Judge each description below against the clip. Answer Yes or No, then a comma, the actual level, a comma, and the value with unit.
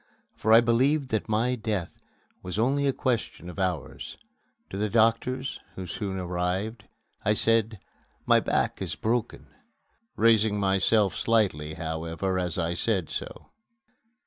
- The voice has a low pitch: Yes, low, 105 Hz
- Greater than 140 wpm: No, slow, 135 wpm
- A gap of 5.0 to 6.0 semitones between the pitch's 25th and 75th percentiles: No, average, 4.0 semitones